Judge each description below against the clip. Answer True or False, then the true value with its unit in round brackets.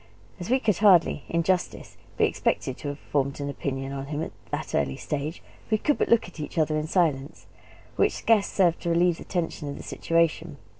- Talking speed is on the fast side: True (210 wpm)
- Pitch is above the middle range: False (160 Hz)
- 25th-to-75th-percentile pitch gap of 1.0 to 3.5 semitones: False (4.0 semitones)